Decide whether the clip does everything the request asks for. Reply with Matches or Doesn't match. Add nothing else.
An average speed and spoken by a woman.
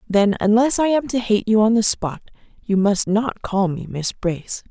Doesn't match